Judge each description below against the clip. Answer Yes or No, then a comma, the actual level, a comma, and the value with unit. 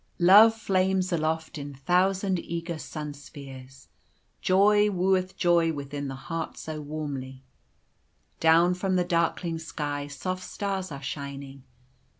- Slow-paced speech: Yes, slow, 120 wpm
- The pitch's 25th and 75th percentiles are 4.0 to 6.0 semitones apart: Yes, average, 4.4 semitones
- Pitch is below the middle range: No, medium, 165 Hz